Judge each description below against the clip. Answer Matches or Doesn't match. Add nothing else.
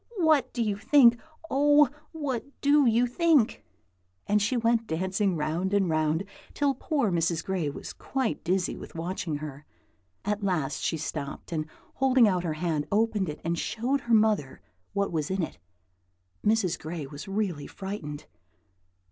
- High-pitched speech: Matches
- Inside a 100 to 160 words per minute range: Matches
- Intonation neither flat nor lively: Doesn't match